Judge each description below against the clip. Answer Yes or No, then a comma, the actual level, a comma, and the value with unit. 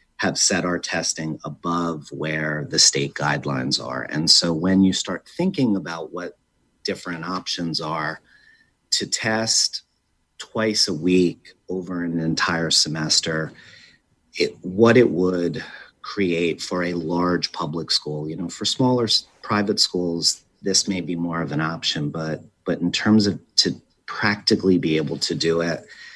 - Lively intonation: No, average, 2.9 semitones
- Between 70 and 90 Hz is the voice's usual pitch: Yes, very low, 85 Hz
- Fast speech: No, average, 150 wpm